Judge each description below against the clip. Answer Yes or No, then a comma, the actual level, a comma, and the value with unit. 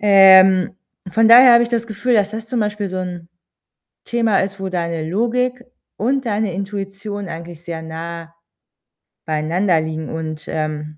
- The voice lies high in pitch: Yes, high, 195 Hz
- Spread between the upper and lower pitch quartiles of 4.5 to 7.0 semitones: Yes, average, 4.8 semitones